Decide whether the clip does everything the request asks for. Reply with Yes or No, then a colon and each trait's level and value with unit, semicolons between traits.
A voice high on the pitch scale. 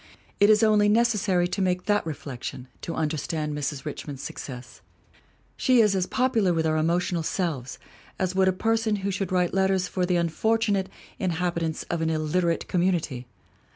No: medium, 180 Hz